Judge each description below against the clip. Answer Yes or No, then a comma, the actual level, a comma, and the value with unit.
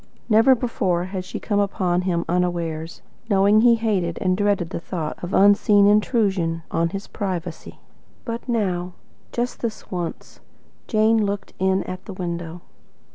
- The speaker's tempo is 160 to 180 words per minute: No, average, 150 wpm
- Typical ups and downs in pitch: Yes, average, 3.2 semitones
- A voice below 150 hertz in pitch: No, high, 190 Hz